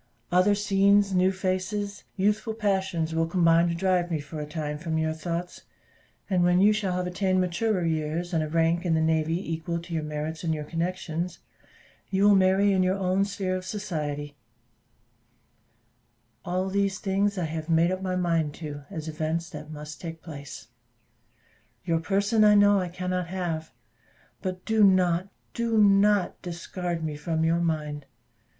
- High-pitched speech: No, medium, 175 Hz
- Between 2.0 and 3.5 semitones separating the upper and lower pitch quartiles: Yes, average, 3.0 semitones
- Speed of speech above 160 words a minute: Yes, average, 170 wpm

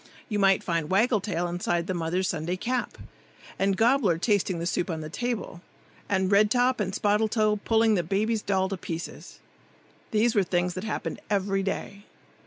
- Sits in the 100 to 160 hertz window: No, high, 195 Hz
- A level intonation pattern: No, average, 3.4 semitones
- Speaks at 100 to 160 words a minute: No, average, 180 wpm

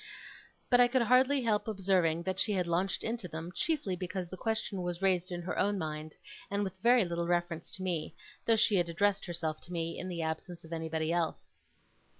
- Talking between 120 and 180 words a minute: No, fast, 205 wpm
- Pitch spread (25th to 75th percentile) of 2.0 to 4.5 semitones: Yes, average, 3.2 semitones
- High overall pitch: No, medium, 180 Hz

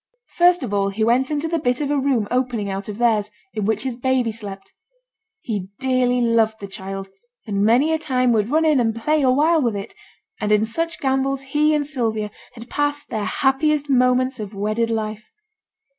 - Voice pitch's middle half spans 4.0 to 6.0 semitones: Yes, average, 4.4 semitones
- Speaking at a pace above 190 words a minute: Yes, average, 200 wpm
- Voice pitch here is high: Yes, high, 245 Hz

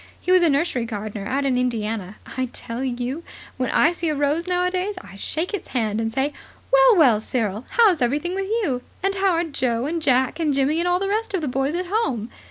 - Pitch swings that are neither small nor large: No, wide, 6.6 semitones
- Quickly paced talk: Yes, fast, 225 wpm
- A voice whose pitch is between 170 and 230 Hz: No, very high, 285 Hz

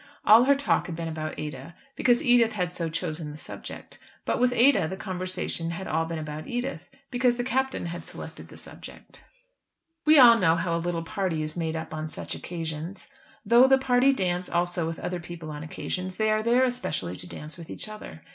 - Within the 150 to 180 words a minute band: No, fast, 205 wpm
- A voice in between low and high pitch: Yes, medium, 180 Hz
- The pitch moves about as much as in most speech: No, wide, 6.8 semitones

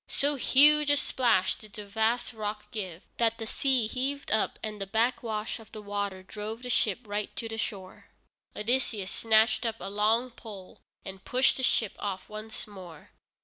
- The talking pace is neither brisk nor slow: Yes, average, 180 wpm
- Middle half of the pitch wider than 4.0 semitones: No, average, 2.8 semitones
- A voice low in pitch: No, high, 220 Hz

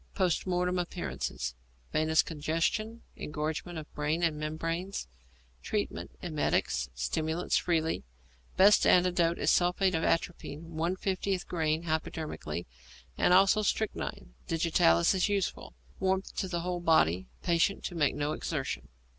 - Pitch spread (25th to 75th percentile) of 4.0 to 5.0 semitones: No, average, 2.8 semitones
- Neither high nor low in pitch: Yes, medium, 165 Hz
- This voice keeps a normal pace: No, slow, 120 wpm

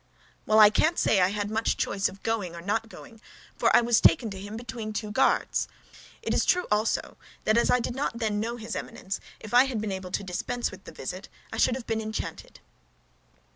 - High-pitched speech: Yes, high, 220 Hz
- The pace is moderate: No, fast, 220 wpm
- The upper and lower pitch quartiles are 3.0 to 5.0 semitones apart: No, narrow, 2.4 semitones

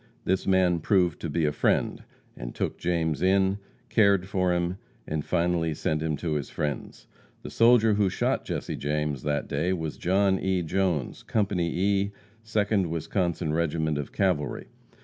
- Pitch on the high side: No, very low, 90 Hz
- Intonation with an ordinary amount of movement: Yes, average, 3.7 semitones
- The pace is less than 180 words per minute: Yes, average, 160 wpm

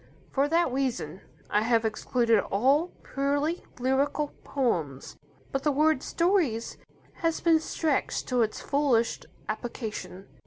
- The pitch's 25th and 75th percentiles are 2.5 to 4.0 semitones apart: No, average, 4.8 semitones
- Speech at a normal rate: No, slow, 120 wpm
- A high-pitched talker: Yes, very high, 265 Hz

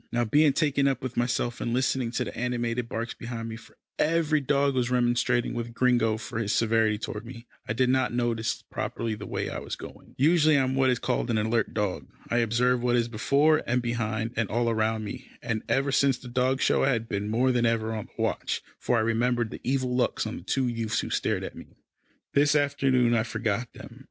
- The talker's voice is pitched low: Yes, low, 120 Hz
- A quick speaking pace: Yes, fast, 230 wpm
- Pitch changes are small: Yes, narrow, 2.2 semitones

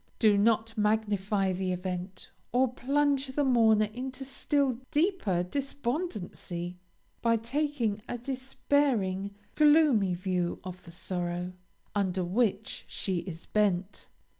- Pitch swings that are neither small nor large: No, wide, 6.0 semitones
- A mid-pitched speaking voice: No, high, 215 Hz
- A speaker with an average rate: No, slow, 115 wpm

